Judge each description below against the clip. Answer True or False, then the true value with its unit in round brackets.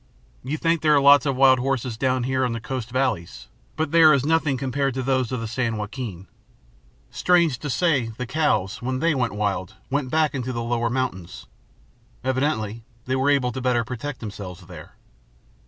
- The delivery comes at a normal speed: True (190 wpm)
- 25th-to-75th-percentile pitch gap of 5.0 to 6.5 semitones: False (3.3 semitones)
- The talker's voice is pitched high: False (130 Hz)